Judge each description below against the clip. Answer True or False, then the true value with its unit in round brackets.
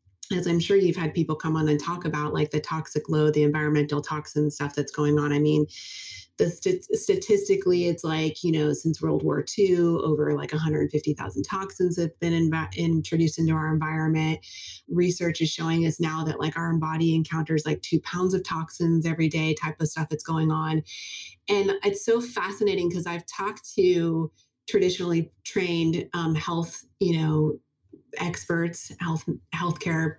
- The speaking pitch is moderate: True (160 Hz)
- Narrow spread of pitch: True (2.0 semitones)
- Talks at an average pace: True (170 wpm)